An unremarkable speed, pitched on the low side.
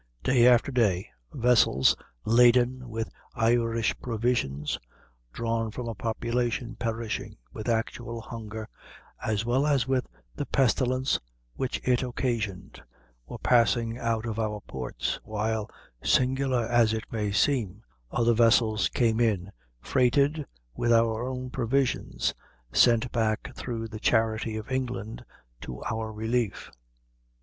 No: slow, 120 wpm; low, 115 Hz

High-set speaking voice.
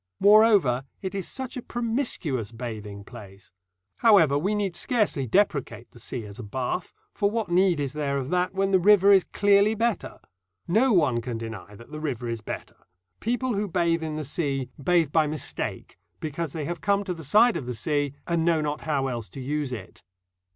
No: medium, 155 Hz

